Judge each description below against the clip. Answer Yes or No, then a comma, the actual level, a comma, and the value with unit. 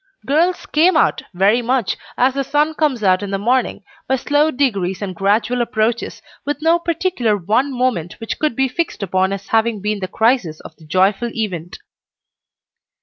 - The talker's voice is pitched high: Yes, high, 235 Hz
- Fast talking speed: No, average, 175 wpm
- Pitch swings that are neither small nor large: No, wide, 5.9 semitones